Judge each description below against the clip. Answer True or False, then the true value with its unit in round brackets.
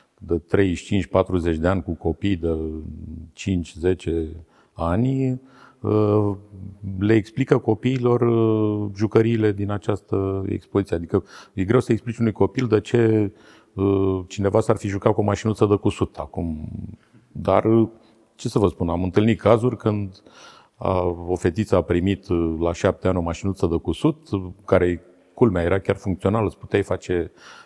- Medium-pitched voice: False (100 Hz)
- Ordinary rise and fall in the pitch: True (3.6 semitones)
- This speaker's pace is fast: False (135 wpm)